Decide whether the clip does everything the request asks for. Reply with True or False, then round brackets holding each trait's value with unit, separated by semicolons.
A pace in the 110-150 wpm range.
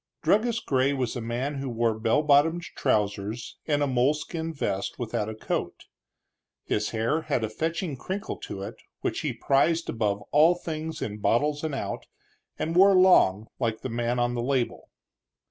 False (170 wpm)